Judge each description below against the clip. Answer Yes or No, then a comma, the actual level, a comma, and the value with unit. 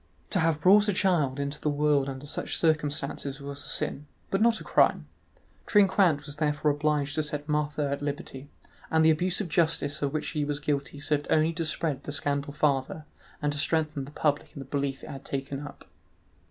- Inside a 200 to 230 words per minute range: Yes, fast, 205 wpm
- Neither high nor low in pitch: Yes, medium, 150 Hz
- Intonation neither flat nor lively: No, narrow, 1.8 semitones